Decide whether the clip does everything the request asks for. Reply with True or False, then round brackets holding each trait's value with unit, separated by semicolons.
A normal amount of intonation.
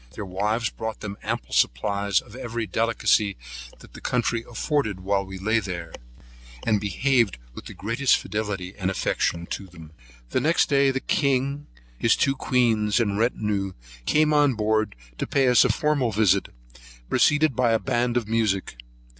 True (4.1 semitones)